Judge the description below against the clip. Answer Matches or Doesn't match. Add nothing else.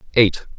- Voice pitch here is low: Matches